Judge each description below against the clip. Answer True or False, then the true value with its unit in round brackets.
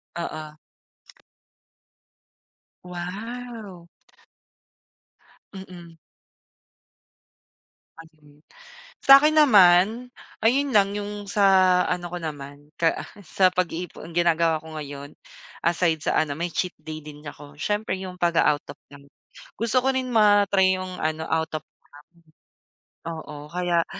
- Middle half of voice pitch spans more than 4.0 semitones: True (4.4 semitones)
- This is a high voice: False (175 Hz)